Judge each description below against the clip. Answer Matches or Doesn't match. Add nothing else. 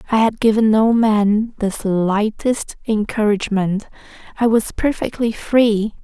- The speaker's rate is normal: Doesn't match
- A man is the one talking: Doesn't match